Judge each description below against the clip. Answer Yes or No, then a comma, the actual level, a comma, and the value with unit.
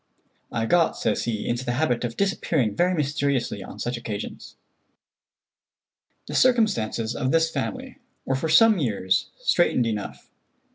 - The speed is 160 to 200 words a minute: No, average, 140 wpm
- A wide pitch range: Yes, wide, 7.0 semitones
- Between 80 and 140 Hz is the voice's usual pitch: Yes, low, 135 Hz